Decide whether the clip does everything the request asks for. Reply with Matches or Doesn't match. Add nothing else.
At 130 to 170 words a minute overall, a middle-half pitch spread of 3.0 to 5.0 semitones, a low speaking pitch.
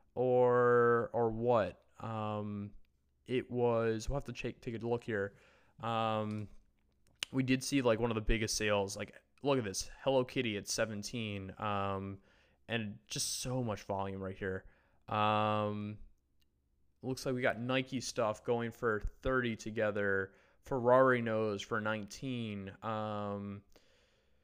Matches